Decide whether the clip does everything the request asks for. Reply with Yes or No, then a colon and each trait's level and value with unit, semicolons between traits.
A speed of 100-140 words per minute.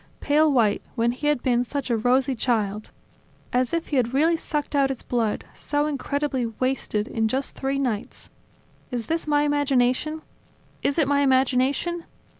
No: average, 165 wpm